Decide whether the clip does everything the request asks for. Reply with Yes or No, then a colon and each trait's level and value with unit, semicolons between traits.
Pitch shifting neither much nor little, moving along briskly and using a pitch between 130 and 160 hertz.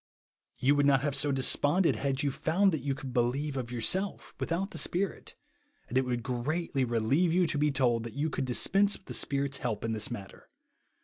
Yes: average, 4.2 semitones; fast, 210 wpm; medium, 140 Hz